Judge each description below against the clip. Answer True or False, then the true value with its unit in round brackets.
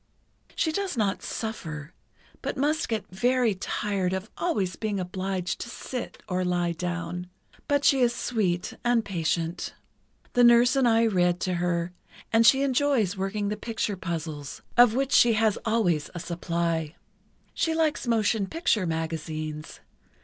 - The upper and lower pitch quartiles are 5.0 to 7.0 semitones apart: True (5.4 semitones)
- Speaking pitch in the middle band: False (200 Hz)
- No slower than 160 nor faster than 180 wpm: False (150 wpm)